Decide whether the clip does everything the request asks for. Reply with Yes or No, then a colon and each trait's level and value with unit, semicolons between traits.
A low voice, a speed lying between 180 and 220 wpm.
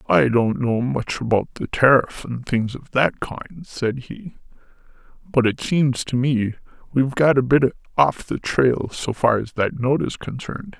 Yes: low, 130 Hz; average, 185 wpm